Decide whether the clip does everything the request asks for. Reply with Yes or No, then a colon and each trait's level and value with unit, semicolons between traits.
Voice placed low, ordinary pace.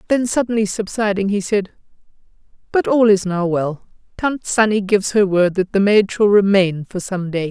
No: high, 200 Hz; average, 185 wpm